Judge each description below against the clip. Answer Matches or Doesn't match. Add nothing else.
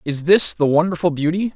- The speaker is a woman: Doesn't match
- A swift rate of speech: Doesn't match